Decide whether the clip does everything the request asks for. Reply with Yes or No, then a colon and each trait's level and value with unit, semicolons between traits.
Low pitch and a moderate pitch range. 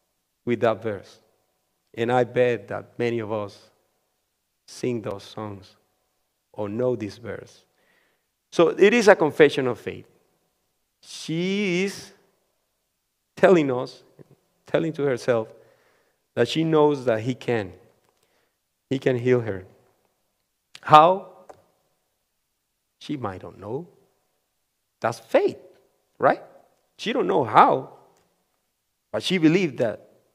No: low, 125 Hz; wide, 5.8 semitones